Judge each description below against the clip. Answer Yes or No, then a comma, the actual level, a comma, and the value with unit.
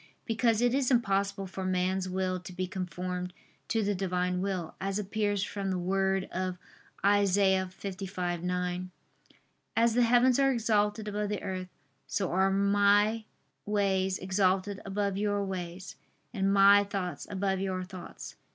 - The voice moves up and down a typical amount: No, narrow, 1.8 semitones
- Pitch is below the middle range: No, high, 195 Hz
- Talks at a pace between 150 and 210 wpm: No, average, 140 wpm